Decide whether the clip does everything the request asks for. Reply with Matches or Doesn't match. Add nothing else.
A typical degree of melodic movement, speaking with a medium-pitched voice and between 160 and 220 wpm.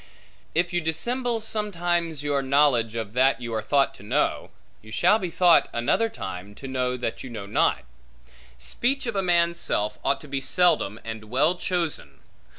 Doesn't match